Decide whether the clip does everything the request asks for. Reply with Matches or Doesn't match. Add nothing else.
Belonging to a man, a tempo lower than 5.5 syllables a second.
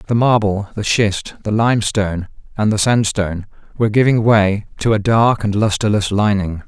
Matches